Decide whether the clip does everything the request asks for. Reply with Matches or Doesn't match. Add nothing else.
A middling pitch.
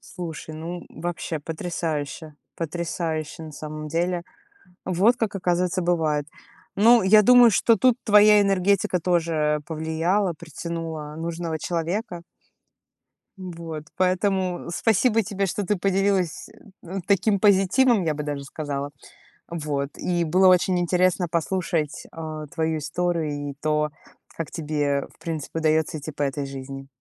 Matches